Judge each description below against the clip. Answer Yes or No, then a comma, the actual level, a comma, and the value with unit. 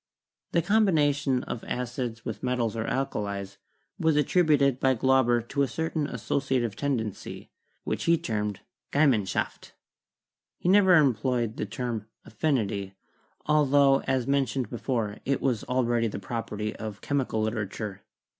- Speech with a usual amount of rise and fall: Yes, average, 4.2 semitones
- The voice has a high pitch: No, low, 125 Hz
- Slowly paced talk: Yes, slow, 125 wpm